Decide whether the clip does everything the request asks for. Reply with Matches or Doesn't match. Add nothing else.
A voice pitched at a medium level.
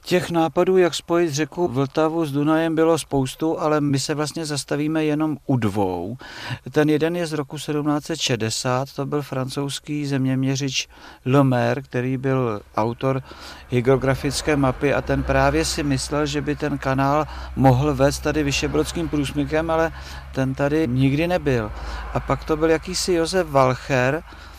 Matches